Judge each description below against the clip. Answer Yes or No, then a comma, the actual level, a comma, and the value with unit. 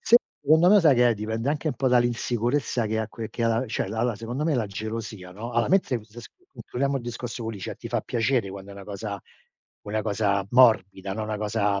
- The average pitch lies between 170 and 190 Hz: No, low, 115 Hz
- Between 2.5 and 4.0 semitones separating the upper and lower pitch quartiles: Yes, average, 2.8 semitones